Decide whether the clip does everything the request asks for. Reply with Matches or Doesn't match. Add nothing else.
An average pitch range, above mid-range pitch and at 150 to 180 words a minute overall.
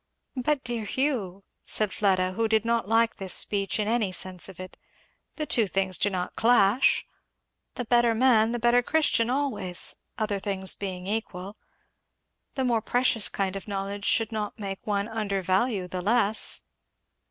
Matches